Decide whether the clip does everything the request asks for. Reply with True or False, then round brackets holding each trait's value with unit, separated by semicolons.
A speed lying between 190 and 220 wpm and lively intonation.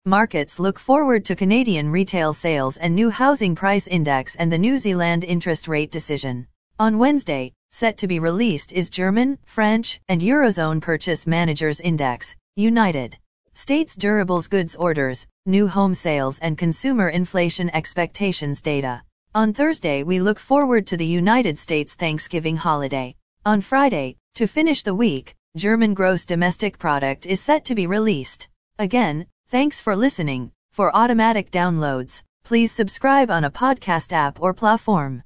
False (150 wpm; 5.7 semitones)